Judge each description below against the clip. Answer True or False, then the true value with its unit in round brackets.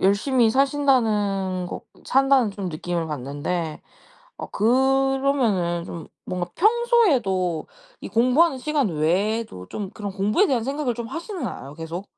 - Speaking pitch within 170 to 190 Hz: False (220 Hz)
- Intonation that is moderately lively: False (7.1 semitones)